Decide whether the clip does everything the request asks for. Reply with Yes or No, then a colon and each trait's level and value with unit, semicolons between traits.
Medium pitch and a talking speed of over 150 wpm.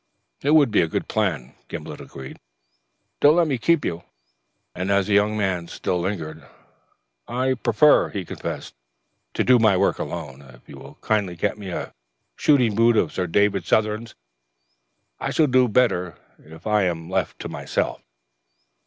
No: low, 105 Hz; average, 165 wpm